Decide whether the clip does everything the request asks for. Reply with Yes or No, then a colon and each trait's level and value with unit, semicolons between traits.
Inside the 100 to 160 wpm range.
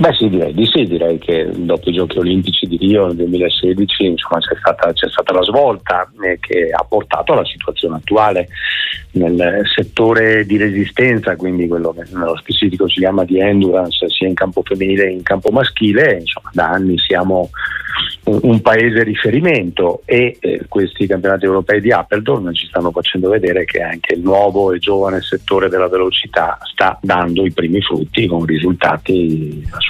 No: fast, 170 wpm